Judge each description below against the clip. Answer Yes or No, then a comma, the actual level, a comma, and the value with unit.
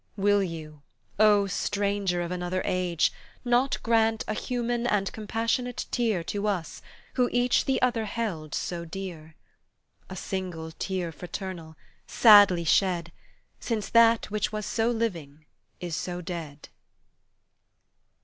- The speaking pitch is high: Yes, high, 195 Hz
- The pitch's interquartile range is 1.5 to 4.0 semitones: No, average, 4.6 semitones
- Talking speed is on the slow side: Yes, slow, 125 wpm